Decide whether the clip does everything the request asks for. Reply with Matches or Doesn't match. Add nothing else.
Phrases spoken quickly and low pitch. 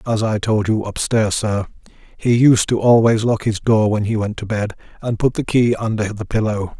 Matches